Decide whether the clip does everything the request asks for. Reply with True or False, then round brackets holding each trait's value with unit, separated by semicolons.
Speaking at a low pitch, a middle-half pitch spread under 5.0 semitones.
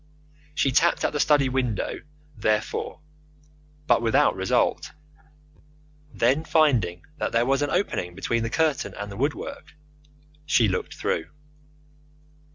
False (130 Hz; 5.5 semitones)